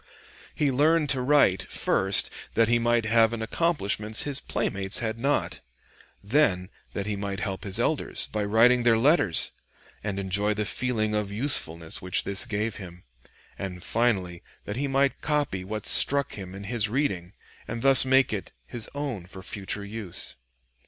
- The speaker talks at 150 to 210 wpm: Yes, average, 165 wpm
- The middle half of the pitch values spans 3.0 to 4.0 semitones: No, average, 4.5 semitones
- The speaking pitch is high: No, low, 110 Hz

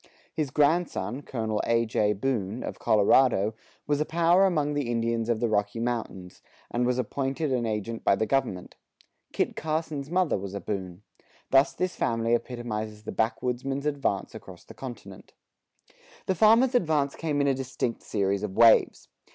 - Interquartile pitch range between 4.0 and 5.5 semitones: Yes, average, 5.0 semitones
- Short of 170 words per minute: Yes, average, 160 wpm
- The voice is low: Yes, low, 120 Hz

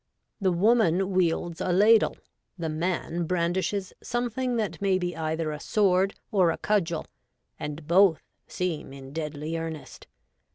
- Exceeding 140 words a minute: No, slow, 135 wpm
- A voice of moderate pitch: Yes, medium, 175 Hz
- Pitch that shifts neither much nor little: Yes, average, 3.3 semitones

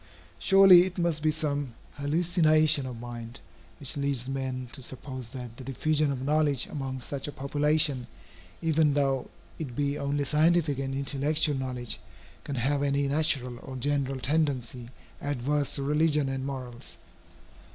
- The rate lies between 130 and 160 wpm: Yes, average, 145 wpm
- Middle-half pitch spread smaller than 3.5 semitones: Yes, narrow, 2.5 semitones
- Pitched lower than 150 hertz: Yes, medium, 140 Hz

